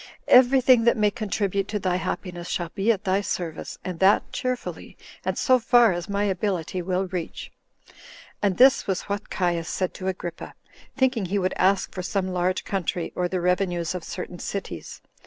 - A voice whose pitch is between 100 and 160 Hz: No, high, 190 Hz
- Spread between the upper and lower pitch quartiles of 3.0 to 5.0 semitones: No, narrow, 2.5 semitones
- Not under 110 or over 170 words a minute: No, average, 180 wpm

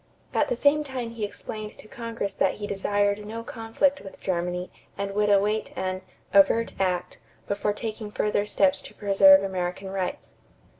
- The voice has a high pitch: Yes, high, 205 Hz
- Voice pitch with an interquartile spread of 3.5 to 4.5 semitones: No, narrow, 2.6 semitones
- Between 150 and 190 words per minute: Yes, average, 160 wpm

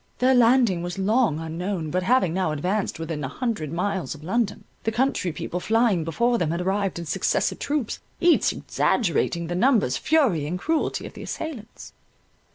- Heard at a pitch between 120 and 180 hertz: No, high, 190 Hz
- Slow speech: No, average, 165 wpm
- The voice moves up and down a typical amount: No, wide, 6.1 semitones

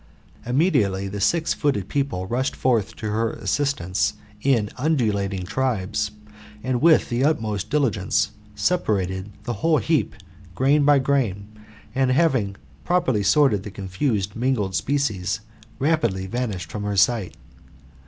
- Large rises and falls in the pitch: Yes, wide, 5.7 semitones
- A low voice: Yes, low, 115 Hz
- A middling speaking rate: No, slow, 125 wpm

